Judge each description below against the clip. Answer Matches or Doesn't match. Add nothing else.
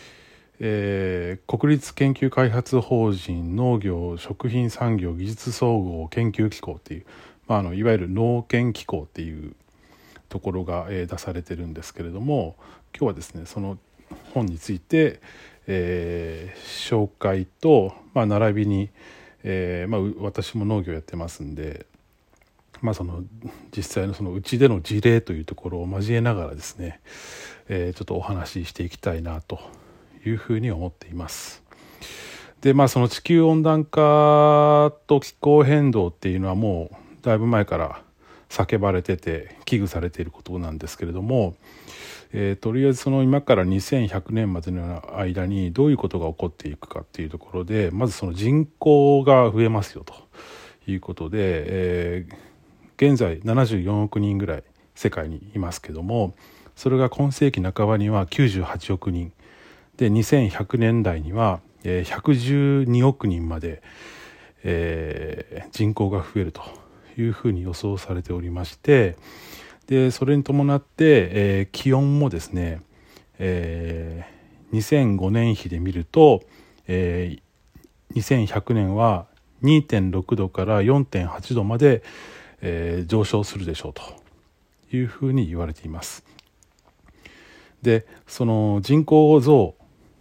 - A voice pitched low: Matches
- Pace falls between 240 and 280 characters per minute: Matches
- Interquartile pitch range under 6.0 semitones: Matches